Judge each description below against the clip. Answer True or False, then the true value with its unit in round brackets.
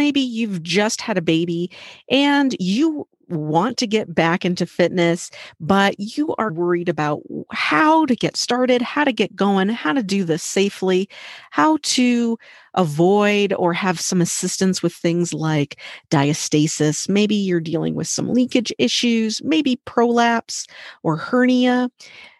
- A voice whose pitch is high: True (195 Hz)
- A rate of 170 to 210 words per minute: False (145 wpm)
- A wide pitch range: True (6.2 semitones)